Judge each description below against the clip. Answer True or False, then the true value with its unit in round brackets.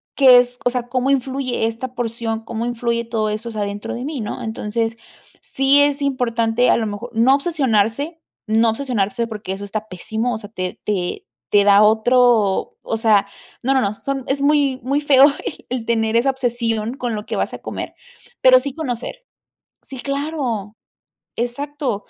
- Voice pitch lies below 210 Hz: False (235 Hz)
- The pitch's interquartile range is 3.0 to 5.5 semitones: True (3.3 semitones)